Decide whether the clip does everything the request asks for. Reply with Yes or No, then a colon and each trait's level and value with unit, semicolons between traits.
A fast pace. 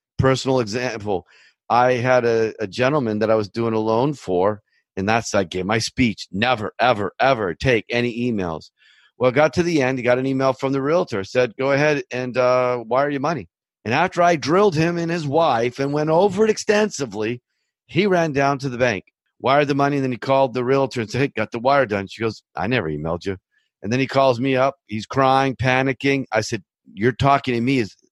Yes: fast, 220 wpm